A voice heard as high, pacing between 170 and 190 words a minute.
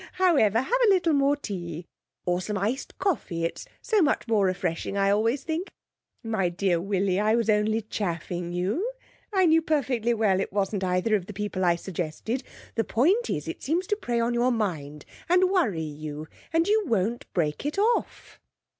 Yes: high, 215 Hz; average, 180 wpm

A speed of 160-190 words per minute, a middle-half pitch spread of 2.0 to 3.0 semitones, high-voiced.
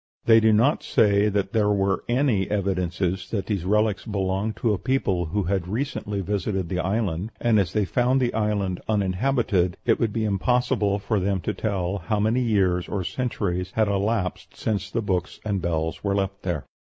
No: average, 185 wpm; average, 2.7 semitones; low, 100 Hz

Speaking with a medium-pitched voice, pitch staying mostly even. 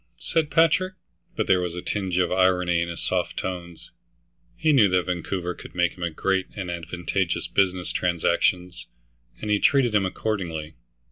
No: very low, 90 Hz; narrow, 2.3 semitones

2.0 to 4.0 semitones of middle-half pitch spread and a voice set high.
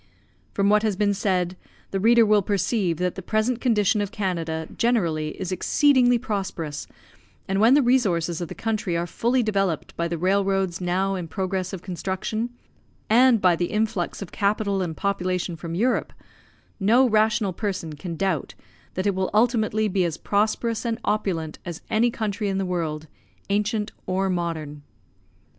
Yes: average, 3.6 semitones; high, 195 Hz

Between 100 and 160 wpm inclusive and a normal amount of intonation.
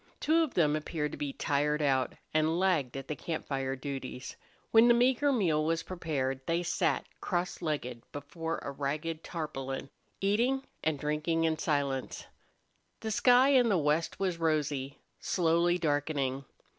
Yes: average, 155 wpm; average, 3.9 semitones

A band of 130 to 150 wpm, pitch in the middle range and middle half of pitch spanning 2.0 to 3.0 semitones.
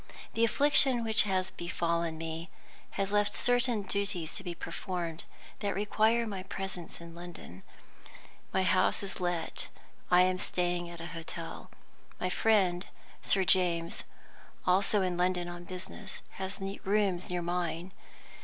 Yes: slow, 135 wpm; medium, 180 Hz; narrow, 2.5 semitones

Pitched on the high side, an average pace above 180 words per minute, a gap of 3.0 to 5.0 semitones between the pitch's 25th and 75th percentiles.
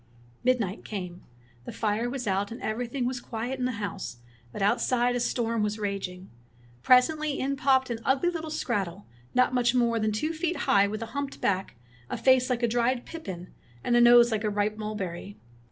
Yes: high, 235 Hz; average, 195 wpm; average, 3.6 semitones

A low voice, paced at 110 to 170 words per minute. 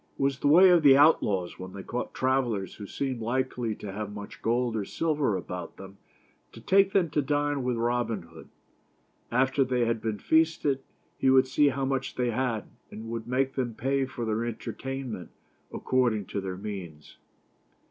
No: low, 125 Hz; average, 180 wpm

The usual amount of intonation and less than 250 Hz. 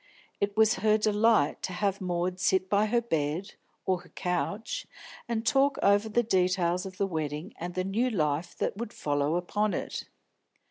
Yes: average, 3.4 semitones; high, 190 Hz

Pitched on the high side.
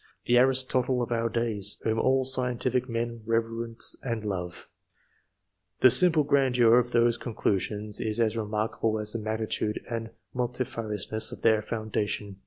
No: low, 115 Hz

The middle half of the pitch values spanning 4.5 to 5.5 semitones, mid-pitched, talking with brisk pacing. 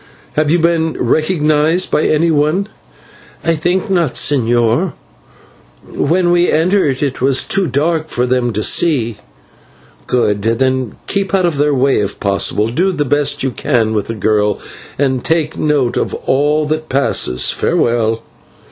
No: average, 5.2 semitones; medium, 145 Hz; average, 145 wpm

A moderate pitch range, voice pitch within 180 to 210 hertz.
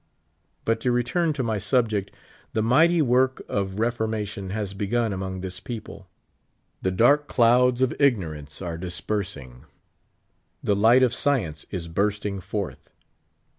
No: average, 4.4 semitones; low, 105 Hz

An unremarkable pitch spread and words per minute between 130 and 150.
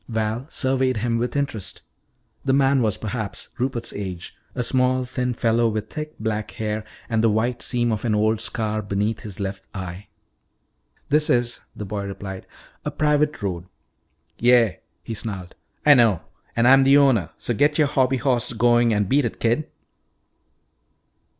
No: average, 3.5 semitones; average, 165 wpm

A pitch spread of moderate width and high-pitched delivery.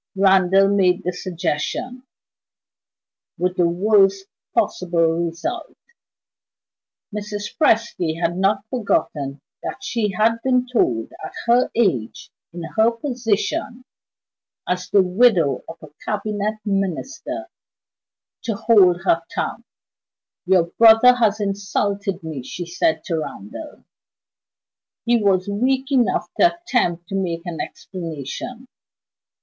Yes: average, 5.0 semitones; high, 200 Hz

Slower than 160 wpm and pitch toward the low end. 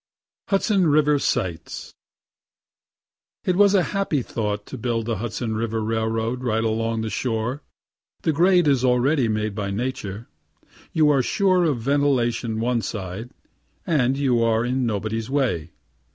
Yes: average, 140 wpm; low, 120 Hz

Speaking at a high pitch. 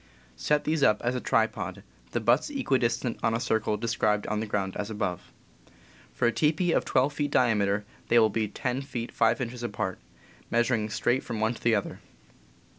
No: low, 115 Hz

